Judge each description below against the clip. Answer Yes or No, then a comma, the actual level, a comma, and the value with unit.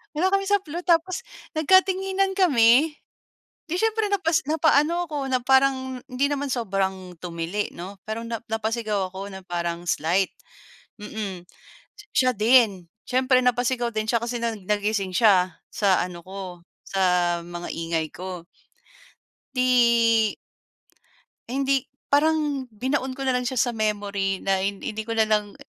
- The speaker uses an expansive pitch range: Yes, wide, 6.0 semitones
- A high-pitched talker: Yes, high, 230 Hz